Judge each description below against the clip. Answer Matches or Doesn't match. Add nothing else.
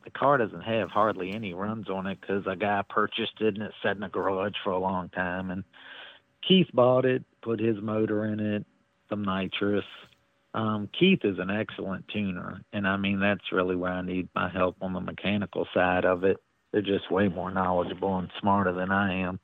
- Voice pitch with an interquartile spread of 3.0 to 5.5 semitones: Doesn't match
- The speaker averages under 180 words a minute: Doesn't match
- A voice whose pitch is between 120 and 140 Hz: Doesn't match